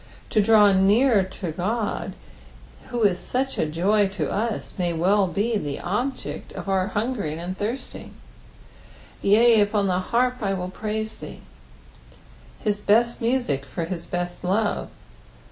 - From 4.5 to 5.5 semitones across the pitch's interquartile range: No, average, 3.6 semitones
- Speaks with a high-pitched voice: Yes, high, 205 Hz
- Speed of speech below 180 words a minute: Yes, average, 145 wpm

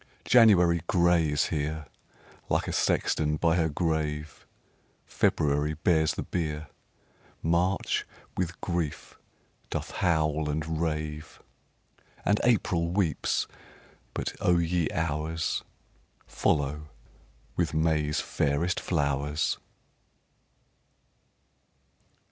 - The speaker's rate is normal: No, slow, 95 wpm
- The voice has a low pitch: Yes, very low, 80 Hz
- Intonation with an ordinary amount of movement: No, narrow, 2.3 semitones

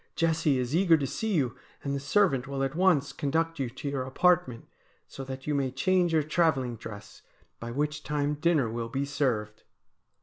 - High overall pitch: No, medium, 140 Hz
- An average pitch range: Yes, average, 3.8 semitones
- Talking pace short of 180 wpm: No, average, 190 wpm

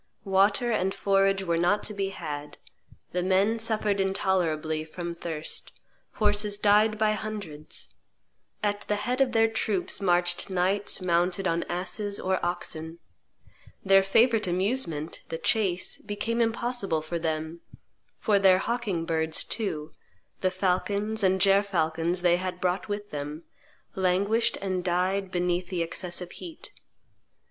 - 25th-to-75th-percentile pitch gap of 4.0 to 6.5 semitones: No, average, 3.0 semitones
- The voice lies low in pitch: No, high, 190 Hz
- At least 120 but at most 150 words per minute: Yes, slow, 135 wpm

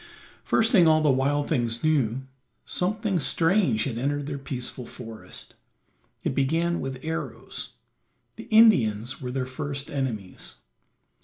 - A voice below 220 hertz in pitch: Yes, medium, 140 Hz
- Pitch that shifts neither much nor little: Yes, average, 4.5 semitones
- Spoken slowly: Yes, slow, 130 wpm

